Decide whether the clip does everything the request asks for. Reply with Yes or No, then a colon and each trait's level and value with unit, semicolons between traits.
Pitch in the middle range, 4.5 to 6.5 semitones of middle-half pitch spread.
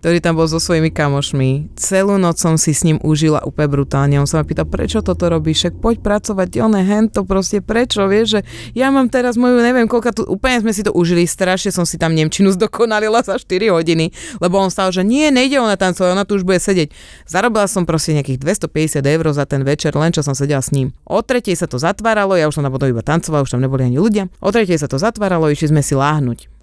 Yes: medium, 175 Hz; average, 5.3 semitones